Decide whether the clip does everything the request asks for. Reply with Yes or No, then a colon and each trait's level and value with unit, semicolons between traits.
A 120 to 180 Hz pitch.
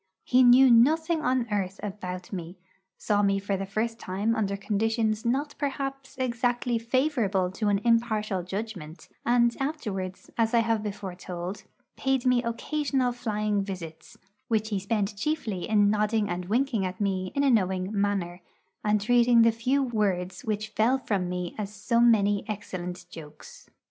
No: high, 215 Hz